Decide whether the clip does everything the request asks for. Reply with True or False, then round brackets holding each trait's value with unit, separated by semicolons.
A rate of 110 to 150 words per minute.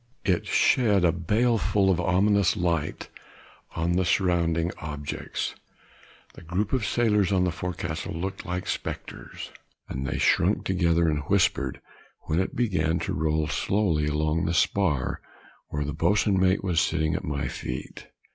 True (145 wpm)